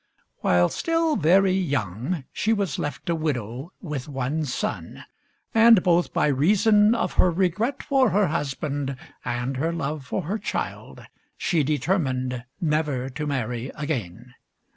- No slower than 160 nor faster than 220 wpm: No, average, 140 wpm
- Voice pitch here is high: No, medium, 150 Hz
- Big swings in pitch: Yes, wide, 6.2 semitones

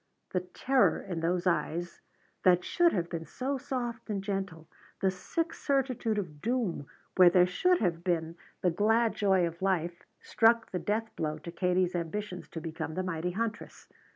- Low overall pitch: No, medium, 185 Hz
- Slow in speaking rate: No, average, 170 wpm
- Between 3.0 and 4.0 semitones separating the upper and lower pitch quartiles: No, average, 4.6 semitones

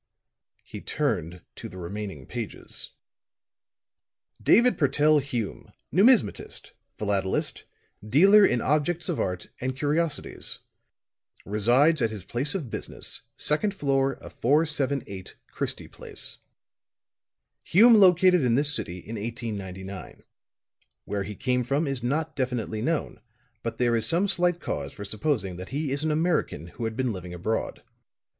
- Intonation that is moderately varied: No, wide, 6.8 semitones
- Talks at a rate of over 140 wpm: No, slow, 135 wpm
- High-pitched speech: No, low, 130 Hz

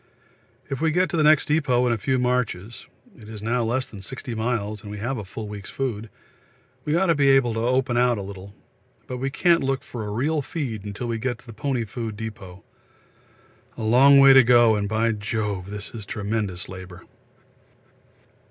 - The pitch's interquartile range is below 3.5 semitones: No, average, 4.1 semitones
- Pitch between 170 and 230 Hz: No, low, 115 Hz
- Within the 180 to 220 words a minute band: Yes, fast, 205 wpm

